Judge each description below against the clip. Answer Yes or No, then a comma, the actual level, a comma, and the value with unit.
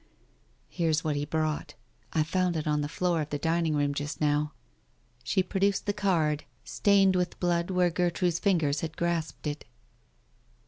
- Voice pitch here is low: No, medium, 165 Hz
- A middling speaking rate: Yes, average, 165 wpm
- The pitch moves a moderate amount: Yes, average, 3.0 semitones